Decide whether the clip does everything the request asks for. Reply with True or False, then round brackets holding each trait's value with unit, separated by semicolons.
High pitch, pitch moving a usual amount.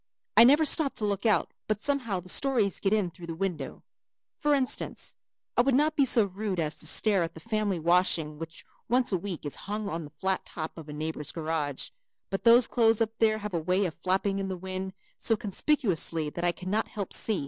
True (195 Hz; 5.0 semitones)